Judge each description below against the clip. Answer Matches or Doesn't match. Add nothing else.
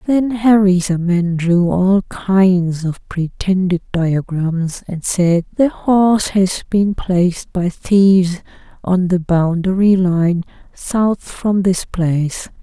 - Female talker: Matches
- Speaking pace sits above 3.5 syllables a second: Doesn't match